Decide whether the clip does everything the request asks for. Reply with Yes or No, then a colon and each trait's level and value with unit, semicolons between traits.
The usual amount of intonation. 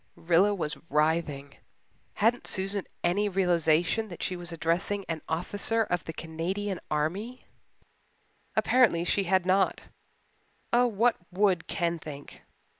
Yes: average, 3.7 semitones